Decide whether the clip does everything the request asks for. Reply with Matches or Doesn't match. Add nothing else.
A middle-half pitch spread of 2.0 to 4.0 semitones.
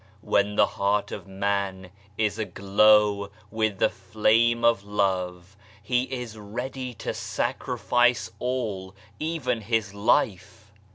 Matches